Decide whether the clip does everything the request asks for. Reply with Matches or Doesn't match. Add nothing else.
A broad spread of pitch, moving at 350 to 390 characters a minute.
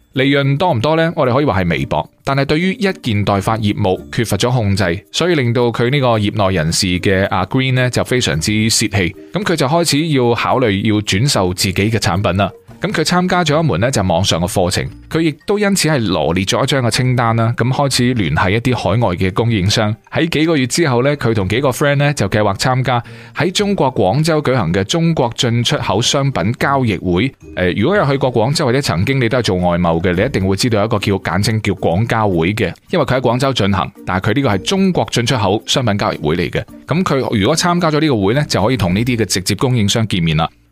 Matches